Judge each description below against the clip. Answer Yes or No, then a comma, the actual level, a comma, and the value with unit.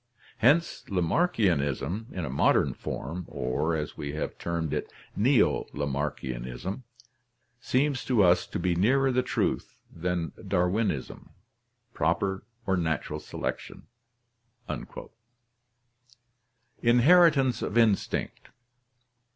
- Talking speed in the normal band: No, slow, 95 wpm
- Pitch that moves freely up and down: Yes, wide, 7.6 semitones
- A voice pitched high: No, very low, 90 Hz